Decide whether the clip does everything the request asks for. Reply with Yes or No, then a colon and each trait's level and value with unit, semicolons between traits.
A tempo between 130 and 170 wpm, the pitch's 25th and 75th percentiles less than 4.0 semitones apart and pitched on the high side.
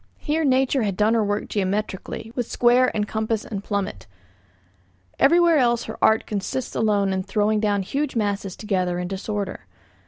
Yes: average, 160 wpm; average, 3.2 semitones; high, 210 Hz